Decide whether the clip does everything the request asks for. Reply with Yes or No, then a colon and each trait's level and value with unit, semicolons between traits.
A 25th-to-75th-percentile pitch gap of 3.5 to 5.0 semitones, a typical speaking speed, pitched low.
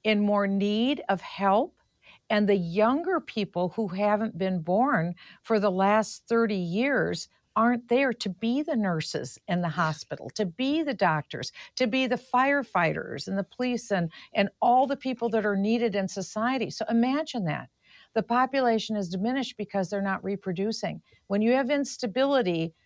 No: average, 4.2 semitones; average, 165 wpm; high, 215 Hz